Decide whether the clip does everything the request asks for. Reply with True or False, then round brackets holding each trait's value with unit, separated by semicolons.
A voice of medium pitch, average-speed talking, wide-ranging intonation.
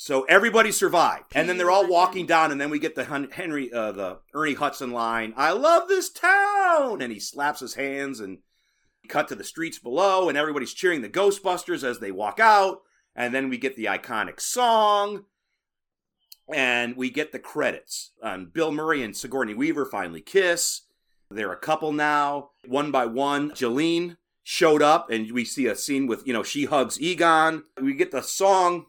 True (155 Hz; 185 wpm; 6.2 semitones)